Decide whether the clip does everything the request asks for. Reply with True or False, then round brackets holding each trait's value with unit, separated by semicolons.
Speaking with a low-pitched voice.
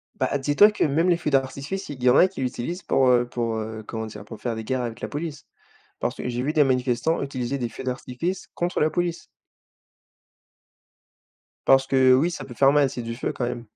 True (130 Hz)